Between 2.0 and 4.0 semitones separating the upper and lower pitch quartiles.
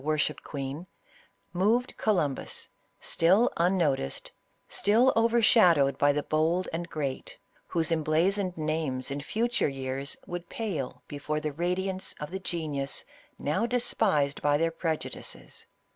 No: average, 4.6 semitones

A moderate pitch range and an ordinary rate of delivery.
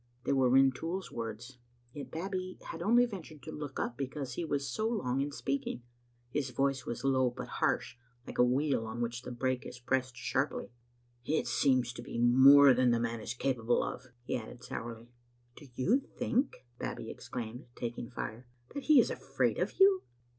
Yes: average, 3.3 semitones; average, 190 wpm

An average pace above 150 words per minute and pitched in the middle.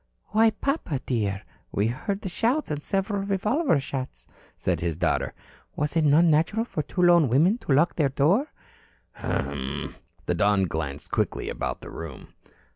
Yes: average, 160 wpm; medium, 150 Hz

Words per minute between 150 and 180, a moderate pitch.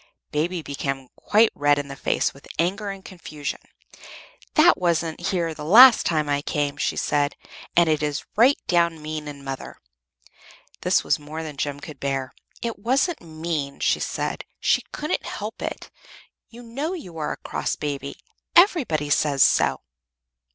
Yes: average, 160 wpm; medium, 155 Hz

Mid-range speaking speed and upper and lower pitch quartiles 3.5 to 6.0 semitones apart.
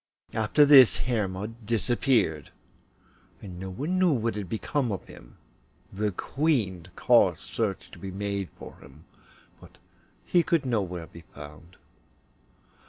No: slow, 130 wpm; average, 5.2 semitones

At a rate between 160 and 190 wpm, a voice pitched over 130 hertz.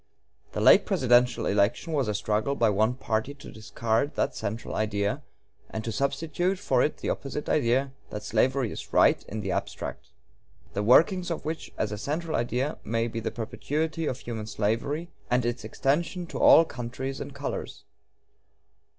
No: average, 170 wpm; low, 125 Hz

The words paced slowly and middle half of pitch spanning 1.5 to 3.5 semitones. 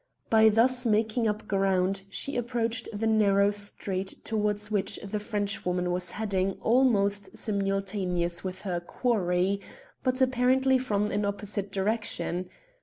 Yes: slow, 125 wpm; narrow, 2.5 semitones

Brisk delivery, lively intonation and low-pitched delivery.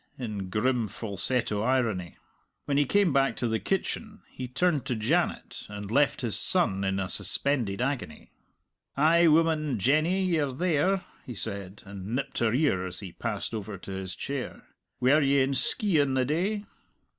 No: average, 165 wpm; wide, 6.7 semitones; low, 130 Hz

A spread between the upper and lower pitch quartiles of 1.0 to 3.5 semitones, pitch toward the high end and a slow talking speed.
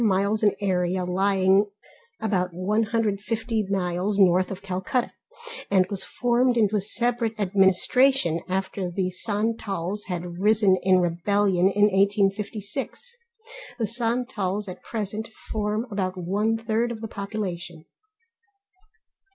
Yes: average, 2.9 semitones; high, 200 Hz; slow, 115 wpm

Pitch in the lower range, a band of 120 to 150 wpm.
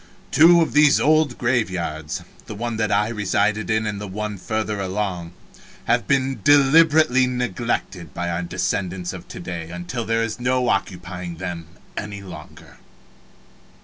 Yes: low, 105 Hz; average, 145 wpm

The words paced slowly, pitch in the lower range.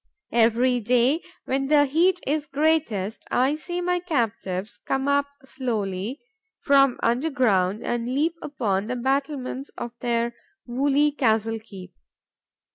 No: slow, 125 wpm; very high, 255 Hz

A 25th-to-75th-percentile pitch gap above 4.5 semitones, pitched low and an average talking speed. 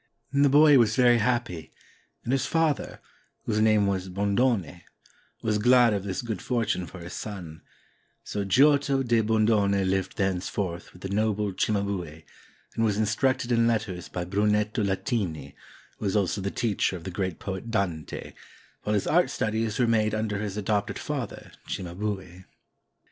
No: average, 3.3 semitones; low, 105 Hz; average, 165 wpm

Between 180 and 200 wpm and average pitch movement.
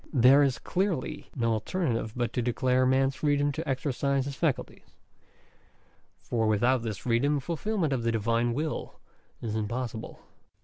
No: average, 140 wpm; average, 3.7 semitones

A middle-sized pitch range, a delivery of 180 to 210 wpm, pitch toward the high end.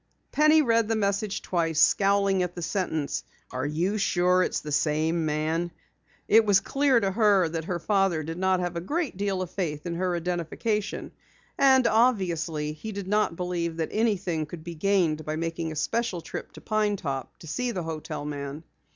No: average, 4.2 semitones; average, 190 wpm; medium, 180 Hz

